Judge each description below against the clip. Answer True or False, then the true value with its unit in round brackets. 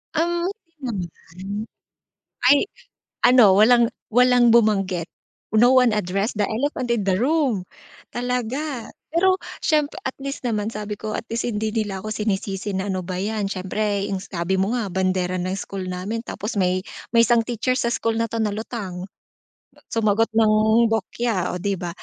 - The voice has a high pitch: True (215 Hz)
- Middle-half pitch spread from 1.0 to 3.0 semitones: False (3.7 semitones)